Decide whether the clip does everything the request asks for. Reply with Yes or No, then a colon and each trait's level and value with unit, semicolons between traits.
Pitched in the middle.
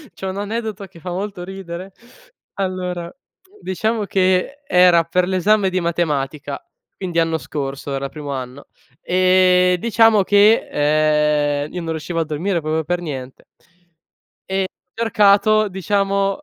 Yes: medium, 180 Hz